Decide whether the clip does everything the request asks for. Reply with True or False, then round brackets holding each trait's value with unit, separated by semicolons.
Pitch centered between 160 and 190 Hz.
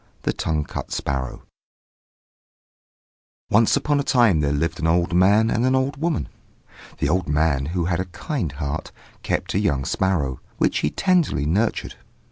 False (90 Hz)